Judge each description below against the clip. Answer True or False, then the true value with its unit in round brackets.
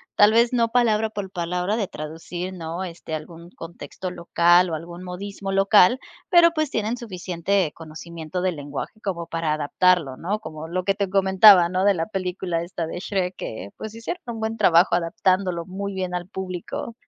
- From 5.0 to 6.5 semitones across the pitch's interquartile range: False (3.2 semitones)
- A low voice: False (185 Hz)